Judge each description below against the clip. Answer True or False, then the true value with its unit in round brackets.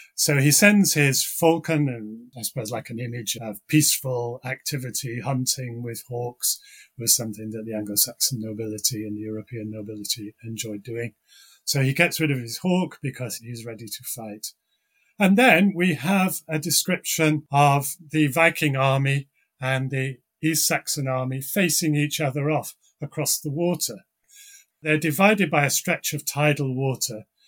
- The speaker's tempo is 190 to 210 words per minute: False (155 wpm)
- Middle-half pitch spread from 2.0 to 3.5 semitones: False (5.2 semitones)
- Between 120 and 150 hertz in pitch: True (140 Hz)